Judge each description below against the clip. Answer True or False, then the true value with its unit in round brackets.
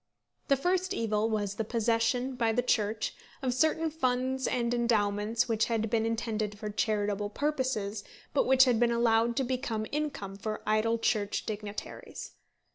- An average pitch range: True (3.0 semitones)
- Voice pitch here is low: False (230 Hz)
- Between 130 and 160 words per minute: True (155 wpm)